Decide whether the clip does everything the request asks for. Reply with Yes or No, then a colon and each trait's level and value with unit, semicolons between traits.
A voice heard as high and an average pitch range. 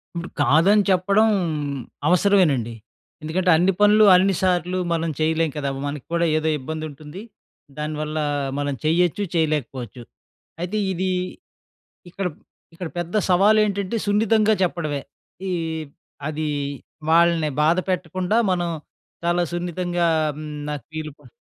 No: medium, 170 Hz; average, 3.3 semitones